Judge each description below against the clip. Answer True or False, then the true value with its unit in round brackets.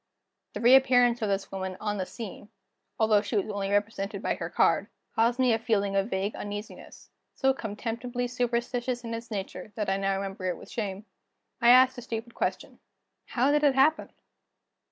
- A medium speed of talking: True (180 wpm)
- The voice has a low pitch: False (225 Hz)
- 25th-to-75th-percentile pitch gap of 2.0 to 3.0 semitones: False (3.6 semitones)